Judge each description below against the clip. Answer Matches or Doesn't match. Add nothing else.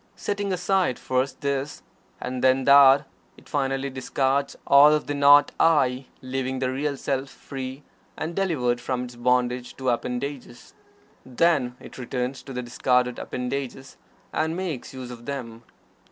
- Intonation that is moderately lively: Doesn't match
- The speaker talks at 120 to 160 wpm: Matches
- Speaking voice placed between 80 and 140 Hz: Matches